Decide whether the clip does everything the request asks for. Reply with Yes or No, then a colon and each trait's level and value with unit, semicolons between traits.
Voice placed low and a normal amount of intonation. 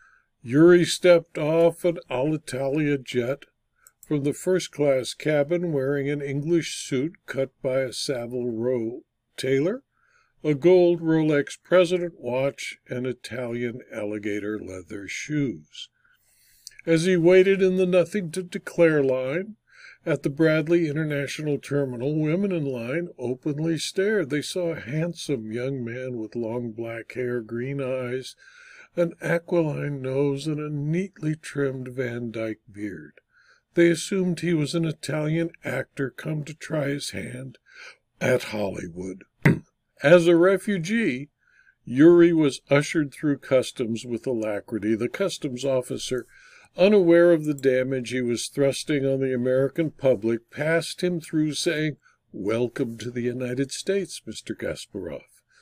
No: medium, 145 Hz; average, 5.0 semitones